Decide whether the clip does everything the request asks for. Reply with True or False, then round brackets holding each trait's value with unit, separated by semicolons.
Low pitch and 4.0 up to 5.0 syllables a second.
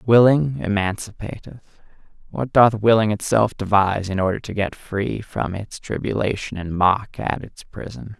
True (105 Hz; 4.6 syllables/s)